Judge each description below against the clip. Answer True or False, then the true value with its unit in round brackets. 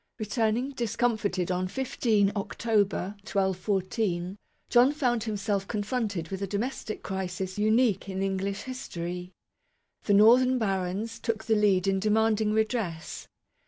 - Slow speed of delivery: True (120 wpm)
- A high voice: True (210 Hz)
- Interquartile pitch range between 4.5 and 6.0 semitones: False (3.0 semitones)